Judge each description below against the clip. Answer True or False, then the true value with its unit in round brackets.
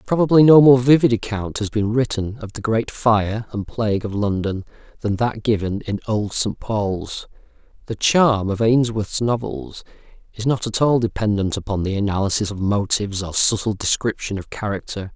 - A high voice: False (110 Hz)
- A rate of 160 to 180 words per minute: True (170 wpm)